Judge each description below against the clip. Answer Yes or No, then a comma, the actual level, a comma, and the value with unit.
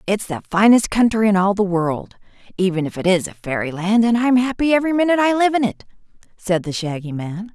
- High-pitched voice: Yes, high, 205 Hz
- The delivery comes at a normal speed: No, fast, 215 wpm